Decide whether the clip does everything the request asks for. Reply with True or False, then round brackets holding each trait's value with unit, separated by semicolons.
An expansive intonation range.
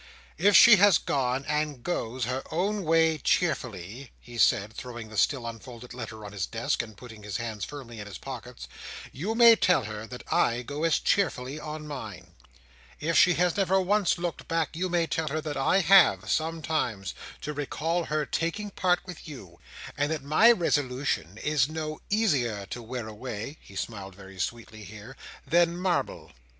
True (6.6 semitones)